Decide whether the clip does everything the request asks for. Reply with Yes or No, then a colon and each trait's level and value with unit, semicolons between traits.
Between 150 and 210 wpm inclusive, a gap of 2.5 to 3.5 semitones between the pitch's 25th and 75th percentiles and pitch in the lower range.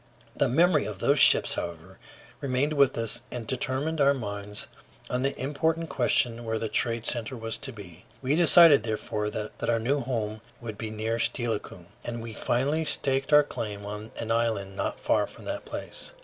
No: average, 185 wpm; average, 4.1 semitones; low, 115 Hz